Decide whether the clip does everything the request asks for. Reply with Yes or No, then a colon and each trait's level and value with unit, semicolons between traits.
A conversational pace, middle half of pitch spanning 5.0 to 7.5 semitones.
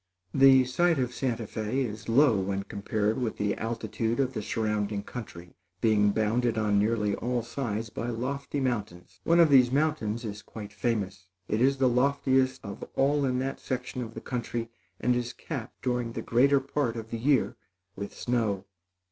No: average, 175 wpm; average, 3.6 semitones